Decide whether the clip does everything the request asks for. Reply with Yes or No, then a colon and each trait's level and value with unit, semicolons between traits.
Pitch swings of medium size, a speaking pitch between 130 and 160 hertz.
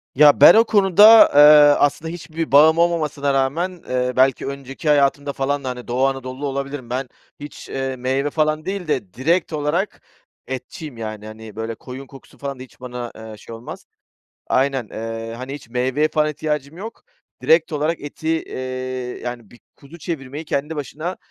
Yes: average, 3.4 semitones; medium, 140 Hz